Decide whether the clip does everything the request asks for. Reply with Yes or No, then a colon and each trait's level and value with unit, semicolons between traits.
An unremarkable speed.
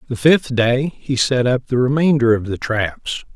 Yes: average, 195 wpm